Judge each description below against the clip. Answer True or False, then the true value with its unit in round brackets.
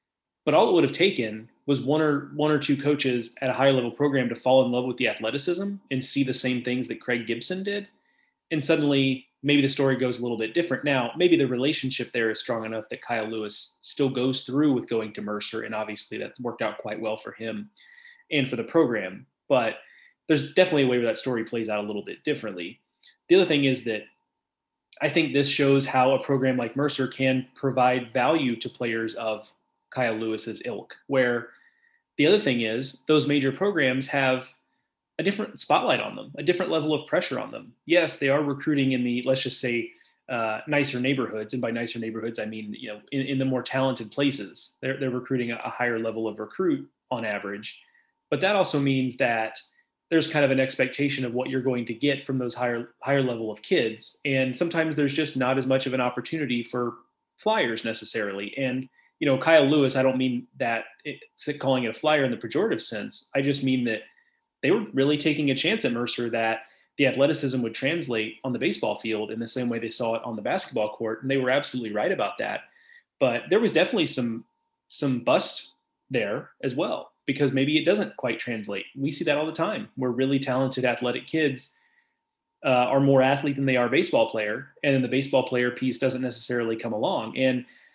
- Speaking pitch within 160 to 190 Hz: False (130 Hz)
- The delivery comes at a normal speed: False (210 wpm)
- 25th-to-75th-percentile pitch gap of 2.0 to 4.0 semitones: True (3.3 semitones)